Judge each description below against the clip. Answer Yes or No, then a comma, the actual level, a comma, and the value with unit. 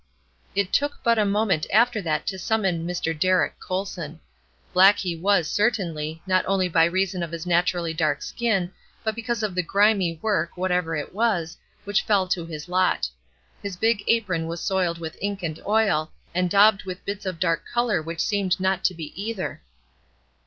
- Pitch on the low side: No, medium, 185 Hz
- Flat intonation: No, average, 3.4 semitones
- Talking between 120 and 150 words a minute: No, average, 180 wpm